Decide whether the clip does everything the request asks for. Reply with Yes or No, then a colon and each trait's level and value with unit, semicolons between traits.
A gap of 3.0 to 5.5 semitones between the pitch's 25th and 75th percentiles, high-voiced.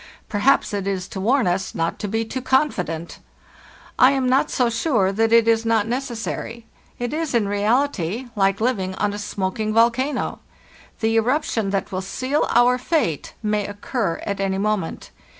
Yes: average, 4.1 semitones; high, 225 Hz